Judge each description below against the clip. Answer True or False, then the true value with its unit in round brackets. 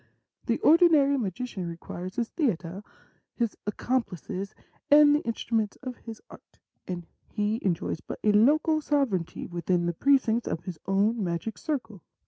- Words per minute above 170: False (145 wpm)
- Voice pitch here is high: True (220 Hz)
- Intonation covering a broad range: True (6.5 semitones)